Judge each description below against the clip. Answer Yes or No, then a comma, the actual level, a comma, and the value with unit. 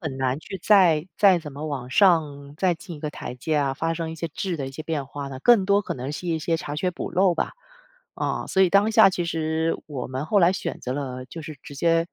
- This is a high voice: No, medium, 160 Hz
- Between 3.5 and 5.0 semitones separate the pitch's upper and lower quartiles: Yes, average, 3.9 semitones